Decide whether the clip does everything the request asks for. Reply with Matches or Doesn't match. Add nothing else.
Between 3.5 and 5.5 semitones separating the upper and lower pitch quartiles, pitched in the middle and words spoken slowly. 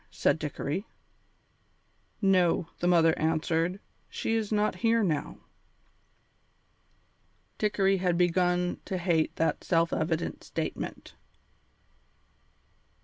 Doesn't match